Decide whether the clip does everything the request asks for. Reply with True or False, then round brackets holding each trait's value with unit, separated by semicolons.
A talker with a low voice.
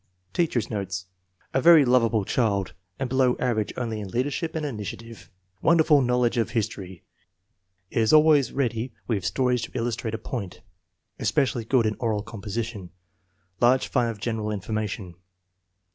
True (115 Hz)